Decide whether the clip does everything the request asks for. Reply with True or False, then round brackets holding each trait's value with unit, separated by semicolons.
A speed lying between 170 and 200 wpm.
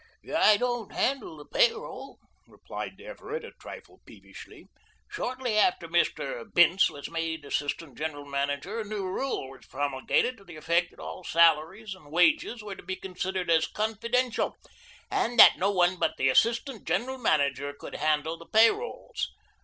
False (160 wpm)